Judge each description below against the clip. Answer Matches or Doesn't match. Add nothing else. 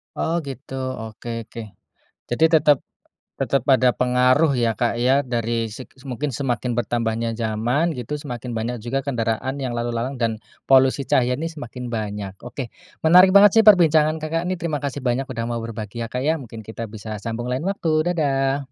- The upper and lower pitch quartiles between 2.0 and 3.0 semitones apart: Doesn't match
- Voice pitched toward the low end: Matches